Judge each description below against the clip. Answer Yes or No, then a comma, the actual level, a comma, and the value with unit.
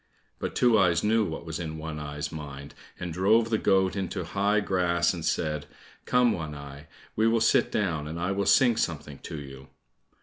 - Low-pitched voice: Yes, very low, 85 Hz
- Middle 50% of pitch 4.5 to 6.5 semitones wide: Yes, average, 5.0 semitones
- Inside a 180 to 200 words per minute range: Yes, average, 195 wpm